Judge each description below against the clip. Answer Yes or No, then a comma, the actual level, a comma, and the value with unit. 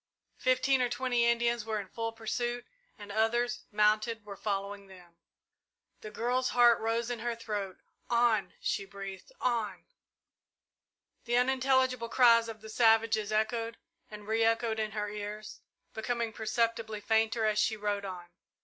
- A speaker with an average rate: Yes, average, 145 wpm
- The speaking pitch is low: No, high, 225 Hz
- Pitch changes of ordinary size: No, narrow, 2.1 semitones